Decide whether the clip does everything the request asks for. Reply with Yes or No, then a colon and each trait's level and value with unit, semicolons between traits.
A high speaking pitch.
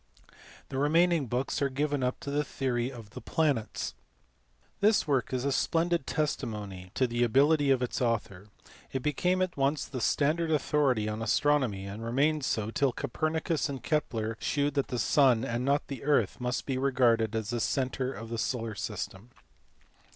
No: low, 130 Hz